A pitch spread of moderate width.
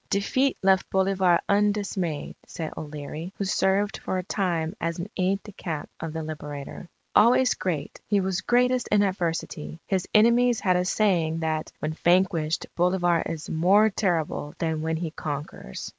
Yes: average, 3.7 semitones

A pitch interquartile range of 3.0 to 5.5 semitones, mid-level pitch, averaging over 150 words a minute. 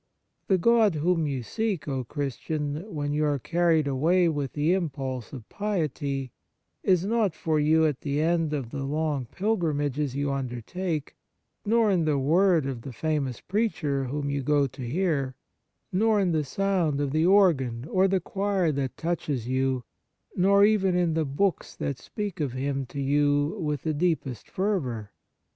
Yes: average, 4.7 semitones; medium, 150 Hz; average, 165 wpm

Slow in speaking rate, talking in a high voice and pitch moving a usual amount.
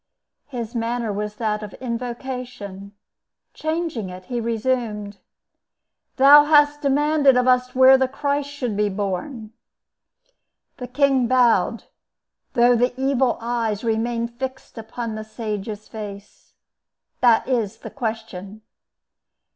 Yes: slow, 115 wpm; high, 235 Hz; average, 3.4 semitones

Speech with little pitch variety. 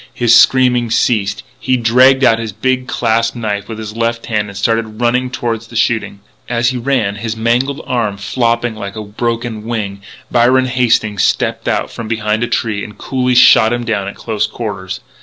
Yes: narrow, 2.1 semitones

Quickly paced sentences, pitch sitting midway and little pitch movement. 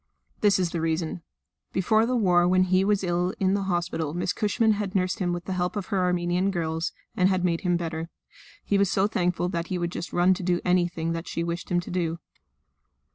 Yes: fast, 225 wpm; medium, 180 Hz; narrow, 1.7 semitones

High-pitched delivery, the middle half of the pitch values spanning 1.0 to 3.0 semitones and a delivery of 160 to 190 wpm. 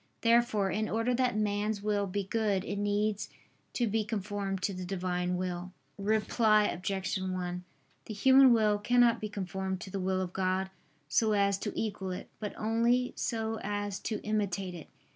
Yes: high, 205 Hz; narrow, 2.4 semitones; average, 170 wpm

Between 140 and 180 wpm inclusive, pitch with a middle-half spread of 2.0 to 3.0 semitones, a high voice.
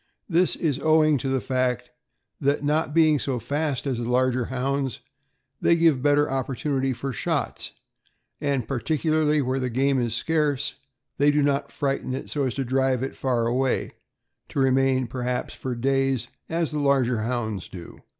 No: average, 170 wpm; narrow, 2.4 semitones; low, 135 Hz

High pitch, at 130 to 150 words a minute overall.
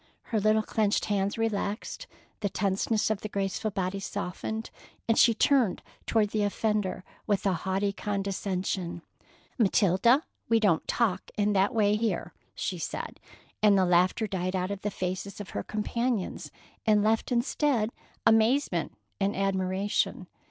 Yes: high, 205 Hz; average, 145 wpm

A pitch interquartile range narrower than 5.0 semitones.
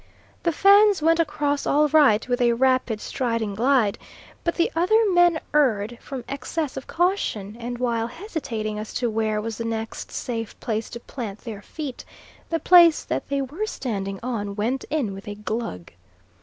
No: wide, 5.6 semitones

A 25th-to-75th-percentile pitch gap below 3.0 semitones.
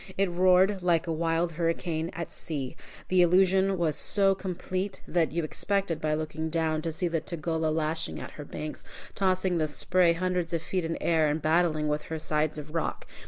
Yes: narrow, 2.6 semitones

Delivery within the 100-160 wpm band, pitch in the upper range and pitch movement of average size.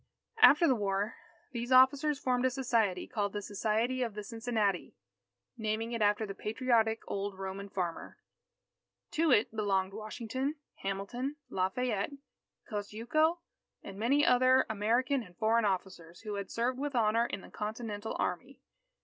Yes: average, 140 wpm; high, 220 Hz; average, 3.9 semitones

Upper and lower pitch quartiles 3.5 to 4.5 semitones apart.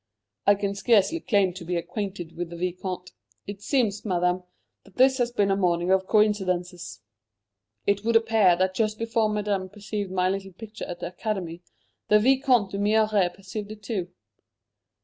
No: average, 2.8 semitones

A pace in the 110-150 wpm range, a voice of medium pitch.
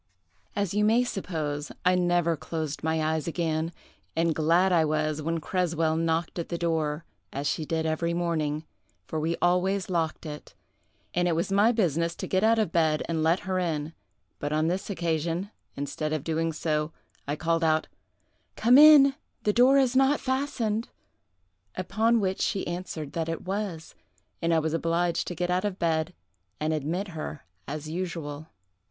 No: average, 170 wpm; medium, 165 Hz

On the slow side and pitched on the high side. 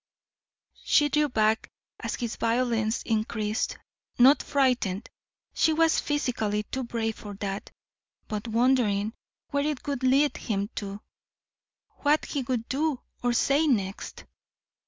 Yes: slow, 125 wpm; high, 240 Hz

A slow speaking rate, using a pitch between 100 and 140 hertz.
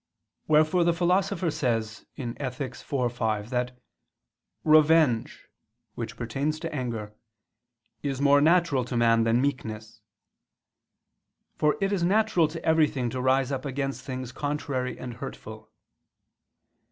Yes: slow, 120 wpm; low, 135 Hz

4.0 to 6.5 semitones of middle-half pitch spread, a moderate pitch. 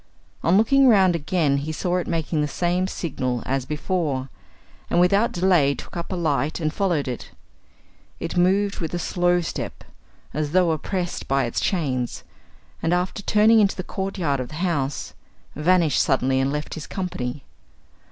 Yes: average, 4.4 semitones; medium, 170 Hz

